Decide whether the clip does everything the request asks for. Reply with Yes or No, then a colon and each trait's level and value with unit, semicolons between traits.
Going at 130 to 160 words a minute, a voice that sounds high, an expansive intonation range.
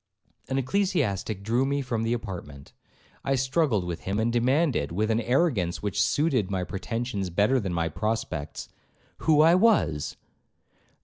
No: average, 145 wpm; low, 115 Hz; wide, 6.2 semitones